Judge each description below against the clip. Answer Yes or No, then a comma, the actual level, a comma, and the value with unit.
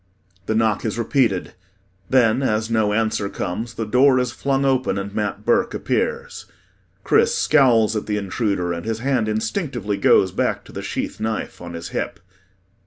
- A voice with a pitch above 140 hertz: No, low, 110 Hz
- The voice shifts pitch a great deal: No, average, 4.0 semitones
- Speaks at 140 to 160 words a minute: No, average, 170 wpm